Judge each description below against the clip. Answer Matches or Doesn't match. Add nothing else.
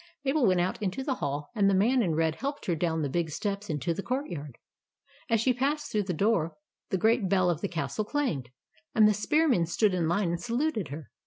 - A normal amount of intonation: Doesn't match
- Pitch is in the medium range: Doesn't match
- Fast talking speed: Matches